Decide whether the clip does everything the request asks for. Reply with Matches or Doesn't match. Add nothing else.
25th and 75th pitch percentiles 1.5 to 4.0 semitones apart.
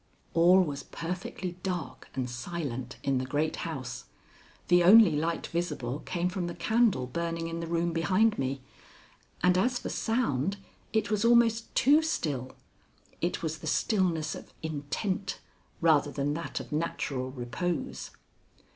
Doesn't match